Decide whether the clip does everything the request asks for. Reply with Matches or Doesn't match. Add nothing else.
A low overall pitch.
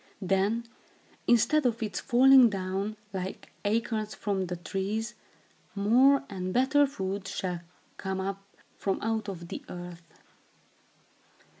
Doesn't match